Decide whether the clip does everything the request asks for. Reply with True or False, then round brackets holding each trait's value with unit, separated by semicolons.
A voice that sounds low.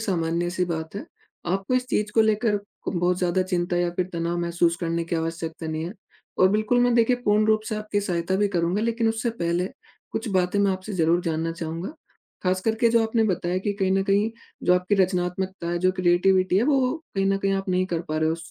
False (185 Hz)